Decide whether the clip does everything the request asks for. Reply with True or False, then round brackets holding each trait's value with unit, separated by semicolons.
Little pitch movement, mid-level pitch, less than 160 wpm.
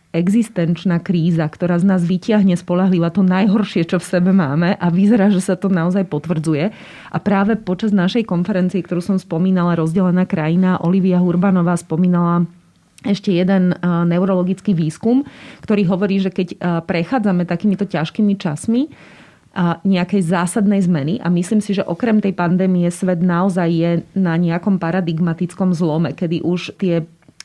True (2.1 semitones; 180 Hz; 145 wpm)